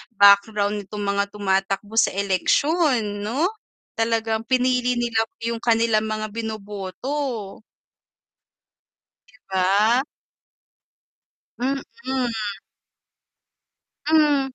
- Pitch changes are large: No, average, 3.5 semitones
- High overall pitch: Yes, high, 220 Hz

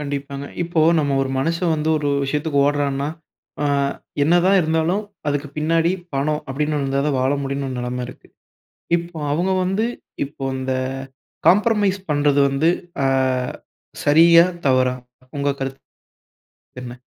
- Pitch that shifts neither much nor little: Yes, average, 3.3 semitones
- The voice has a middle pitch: Yes, medium, 145 Hz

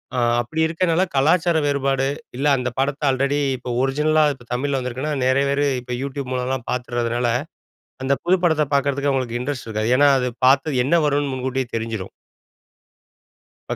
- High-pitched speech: No, low, 135 Hz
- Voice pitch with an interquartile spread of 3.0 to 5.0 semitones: No, narrow, 2.4 semitones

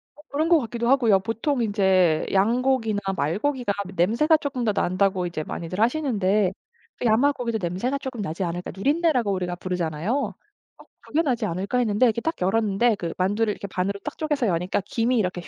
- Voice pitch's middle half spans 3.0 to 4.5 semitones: No, average, 5.3 semitones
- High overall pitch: Yes, high, 215 Hz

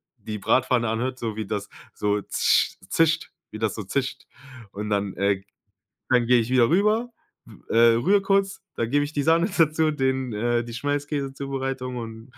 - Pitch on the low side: Yes, low, 125 Hz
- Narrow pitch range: No, average, 4.5 semitones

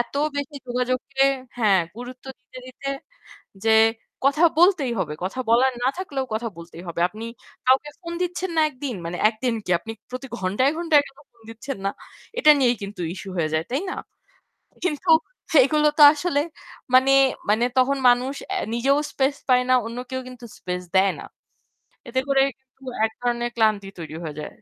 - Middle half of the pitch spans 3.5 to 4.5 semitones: Yes, average, 3.9 semitones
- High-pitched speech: Yes, very high, 255 Hz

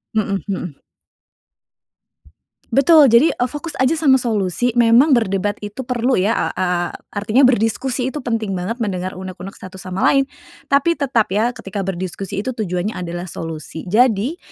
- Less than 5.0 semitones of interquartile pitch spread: No, average, 5.3 semitones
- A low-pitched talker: No, high, 220 Hz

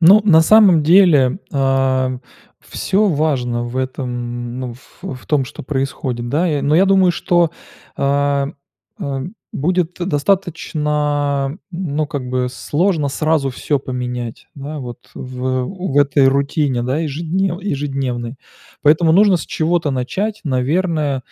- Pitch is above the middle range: No, medium, 145 Hz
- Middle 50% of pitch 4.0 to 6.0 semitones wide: Yes, average, 4.4 semitones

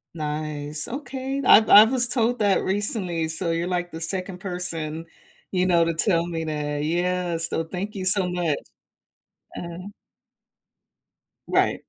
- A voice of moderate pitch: Yes, medium, 175 Hz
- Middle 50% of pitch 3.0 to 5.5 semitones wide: Yes, average, 3.3 semitones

